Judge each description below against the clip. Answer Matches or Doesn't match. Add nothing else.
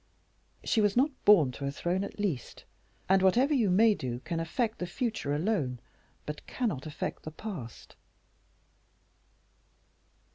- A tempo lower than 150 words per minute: Matches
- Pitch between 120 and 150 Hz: Doesn't match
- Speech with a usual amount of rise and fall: Doesn't match